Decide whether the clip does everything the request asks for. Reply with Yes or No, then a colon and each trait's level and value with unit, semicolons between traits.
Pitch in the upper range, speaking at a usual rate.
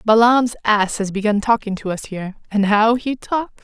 Yes: high, 220 Hz; average, 180 wpm